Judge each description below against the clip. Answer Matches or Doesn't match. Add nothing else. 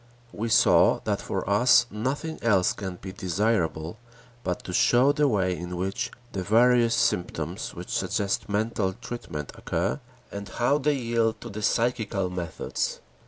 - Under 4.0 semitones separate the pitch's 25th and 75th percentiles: Doesn't match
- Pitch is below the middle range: Matches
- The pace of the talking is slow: Doesn't match